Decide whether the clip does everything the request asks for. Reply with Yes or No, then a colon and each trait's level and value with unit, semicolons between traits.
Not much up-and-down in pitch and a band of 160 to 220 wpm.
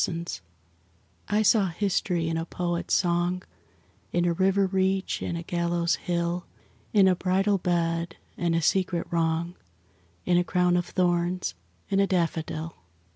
No: narrow, 1.6 semitones; average, 145 wpm